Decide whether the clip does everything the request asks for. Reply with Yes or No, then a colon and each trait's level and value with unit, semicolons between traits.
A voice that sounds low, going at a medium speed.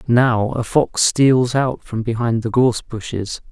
Yes: low, 120 Hz; average, 170 wpm